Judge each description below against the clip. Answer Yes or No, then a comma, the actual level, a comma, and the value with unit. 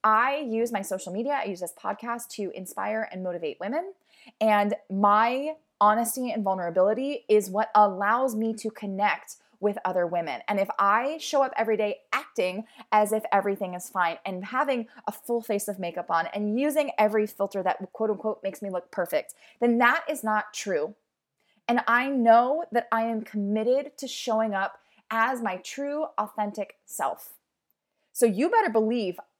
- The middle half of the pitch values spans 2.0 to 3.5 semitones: Yes, average, 2.9 semitones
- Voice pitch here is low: No, high, 215 Hz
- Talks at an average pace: Yes, average, 170 wpm